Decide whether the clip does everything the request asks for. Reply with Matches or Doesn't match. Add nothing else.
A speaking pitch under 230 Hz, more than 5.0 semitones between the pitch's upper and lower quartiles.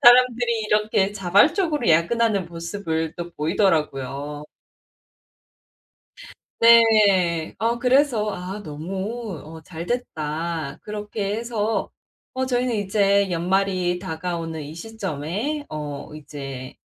Matches